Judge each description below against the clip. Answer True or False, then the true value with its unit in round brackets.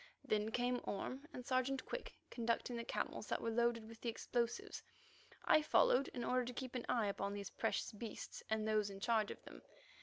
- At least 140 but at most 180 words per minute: False (200 wpm)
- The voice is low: False (235 Hz)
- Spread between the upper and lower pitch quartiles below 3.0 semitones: True (2.5 semitones)